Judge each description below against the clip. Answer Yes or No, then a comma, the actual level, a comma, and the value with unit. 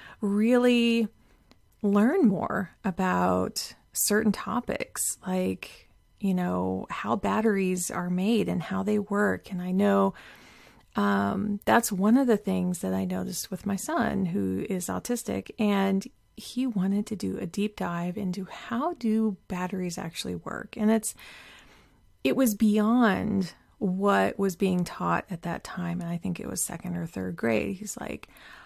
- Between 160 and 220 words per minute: No, average, 150 wpm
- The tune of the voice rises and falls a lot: No, average, 3.1 semitones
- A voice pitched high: Yes, high, 195 Hz